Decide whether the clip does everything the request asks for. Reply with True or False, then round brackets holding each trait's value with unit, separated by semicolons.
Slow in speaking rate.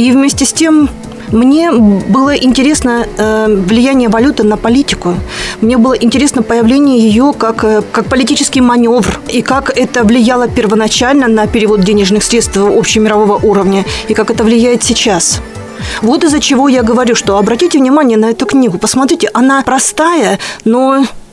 False (145 wpm)